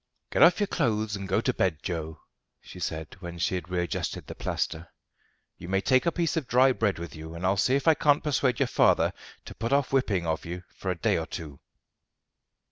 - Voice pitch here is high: No, very low, 95 Hz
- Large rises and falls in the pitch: Yes, wide, 7.4 semitones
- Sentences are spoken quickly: Yes, fast, 220 wpm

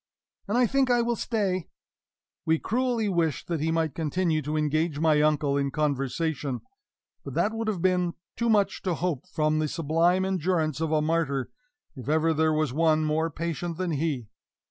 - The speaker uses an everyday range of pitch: Yes, average, 3.3 semitones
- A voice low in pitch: No, medium, 160 Hz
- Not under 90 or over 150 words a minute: No, average, 180 wpm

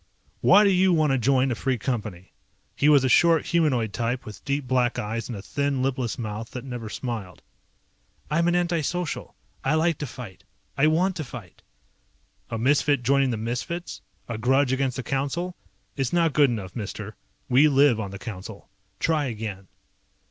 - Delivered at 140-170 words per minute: No, average, 180 wpm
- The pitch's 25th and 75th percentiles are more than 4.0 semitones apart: Yes, average, 4.7 semitones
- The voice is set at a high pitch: No, low, 130 Hz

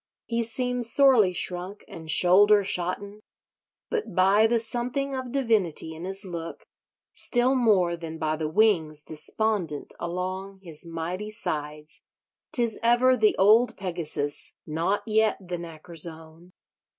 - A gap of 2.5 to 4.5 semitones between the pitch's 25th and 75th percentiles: No, average, 5.1 semitones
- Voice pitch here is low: No, high, 190 Hz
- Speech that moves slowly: Yes, slow, 125 wpm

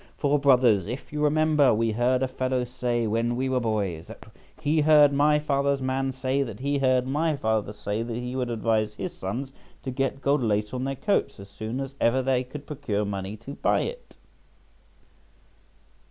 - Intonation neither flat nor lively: Yes, average, 3.6 semitones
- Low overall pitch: Yes, low, 130 Hz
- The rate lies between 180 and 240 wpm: Yes, average, 190 wpm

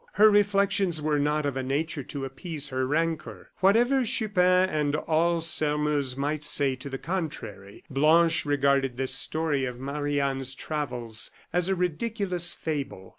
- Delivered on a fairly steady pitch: No, average, 4.2 semitones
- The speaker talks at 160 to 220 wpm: No, average, 150 wpm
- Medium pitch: Yes, medium, 150 Hz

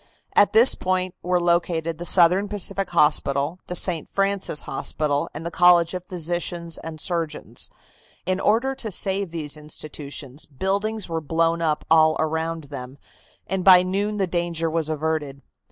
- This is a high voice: No, medium, 170 Hz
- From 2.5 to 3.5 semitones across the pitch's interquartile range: Yes, average, 2.9 semitones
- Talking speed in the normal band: Yes, average, 155 wpm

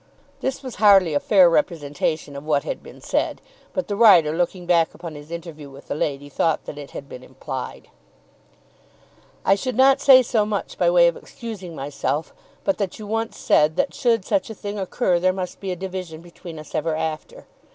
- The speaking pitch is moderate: Yes, medium, 175 Hz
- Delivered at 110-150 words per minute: No, average, 200 wpm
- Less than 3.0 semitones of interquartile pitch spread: No, wide, 5.6 semitones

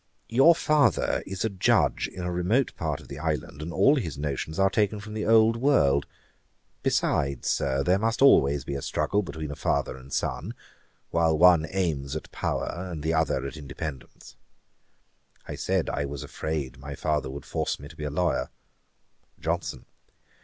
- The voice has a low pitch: Yes, very low, 80 Hz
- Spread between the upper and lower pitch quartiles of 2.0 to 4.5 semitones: No, wide, 5.4 semitones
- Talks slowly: No, average, 175 wpm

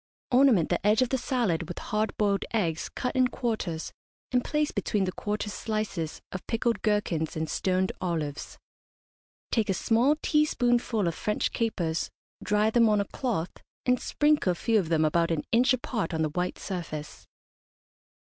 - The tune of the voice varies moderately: No, wide, 5.8 semitones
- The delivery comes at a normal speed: Yes, average, 170 wpm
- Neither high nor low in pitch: No, high, 210 Hz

